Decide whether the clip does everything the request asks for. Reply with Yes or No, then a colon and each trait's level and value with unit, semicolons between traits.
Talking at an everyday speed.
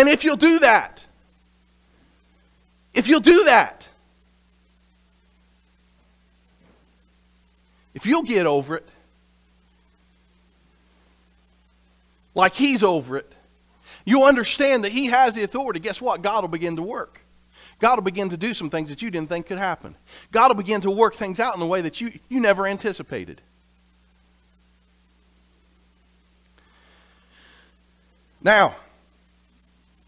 No: slow, 120 wpm